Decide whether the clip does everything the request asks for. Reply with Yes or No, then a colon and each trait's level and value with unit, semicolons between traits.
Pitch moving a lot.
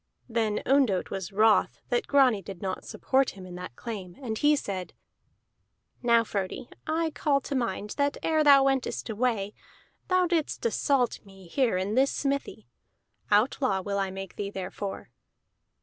Yes: wide, 6.0 semitones